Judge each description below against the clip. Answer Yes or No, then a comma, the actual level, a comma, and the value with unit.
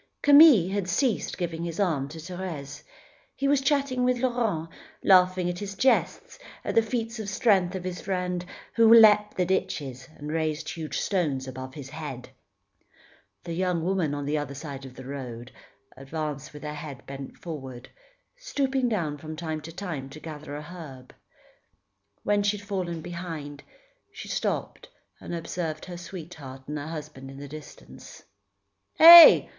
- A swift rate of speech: No, average, 160 wpm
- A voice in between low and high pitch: Yes, medium, 165 Hz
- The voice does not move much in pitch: No, average, 5.3 semitones